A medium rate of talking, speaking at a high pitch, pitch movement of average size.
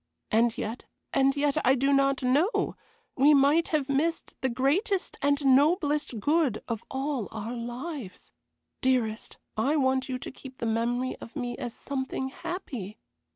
Yes: average, 155 wpm; very high, 265 Hz; average, 3.1 semitones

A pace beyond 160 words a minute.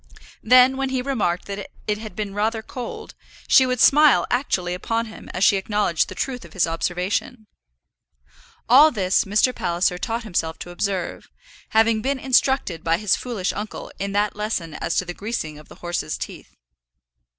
Yes: average, 175 wpm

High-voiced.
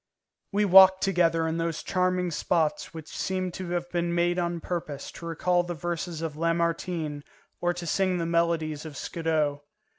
No: medium, 170 Hz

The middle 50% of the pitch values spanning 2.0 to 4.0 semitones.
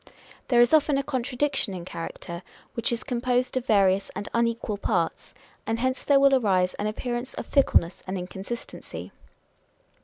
No: average, 4.7 semitones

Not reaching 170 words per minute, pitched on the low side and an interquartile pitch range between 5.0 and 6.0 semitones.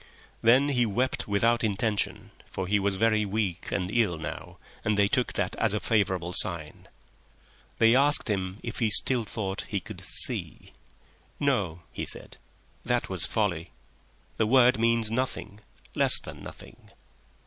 No: average, 150 wpm; low, 105 Hz; average, 3.4 semitones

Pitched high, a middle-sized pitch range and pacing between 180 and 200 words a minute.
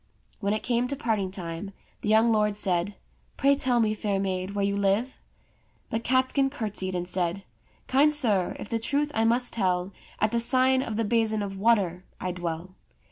Yes: high, 210 Hz; average, 4.0 semitones; average, 195 wpm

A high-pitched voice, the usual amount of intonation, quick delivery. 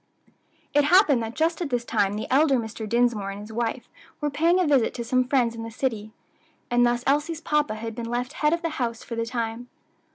Yes: high, 245 Hz; average, 4.3 semitones; fast, 225 wpm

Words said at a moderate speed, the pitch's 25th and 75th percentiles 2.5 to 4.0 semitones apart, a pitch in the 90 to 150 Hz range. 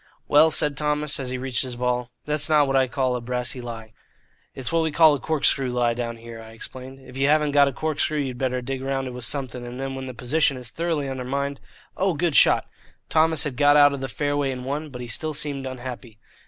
No: fast, 235 wpm; average, 2.8 semitones; low, 135 Hz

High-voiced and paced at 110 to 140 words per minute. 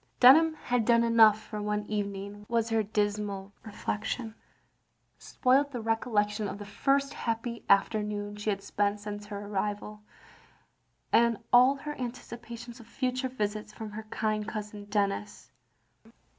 Yes: high, 215 Hz; slow, 135 wpm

